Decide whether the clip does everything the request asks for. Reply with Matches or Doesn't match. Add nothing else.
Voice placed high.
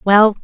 Matches